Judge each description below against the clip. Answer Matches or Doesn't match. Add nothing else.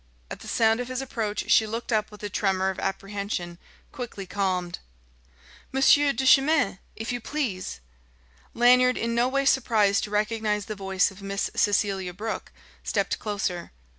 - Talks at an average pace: Matches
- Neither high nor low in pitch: Doesn't match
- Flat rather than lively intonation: Doesn't match